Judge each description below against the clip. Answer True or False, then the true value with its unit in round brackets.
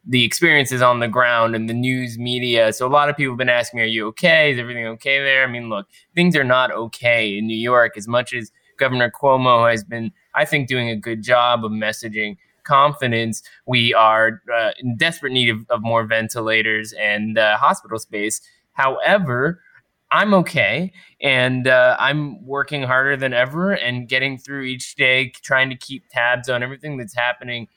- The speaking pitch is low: True (125 Hz)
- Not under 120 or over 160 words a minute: False (190 wpm)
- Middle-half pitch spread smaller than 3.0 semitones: True (2.6 semitones)